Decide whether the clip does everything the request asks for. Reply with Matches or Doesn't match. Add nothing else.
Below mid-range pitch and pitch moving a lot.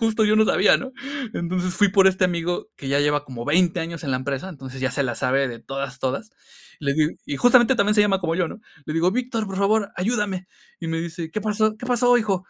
Doesn't match